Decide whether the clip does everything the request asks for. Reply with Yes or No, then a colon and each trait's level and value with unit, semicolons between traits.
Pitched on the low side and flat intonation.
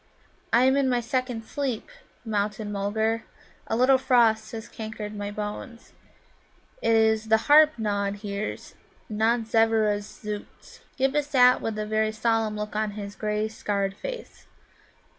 No: high, 220 Hz; narrow, 2.2 semitones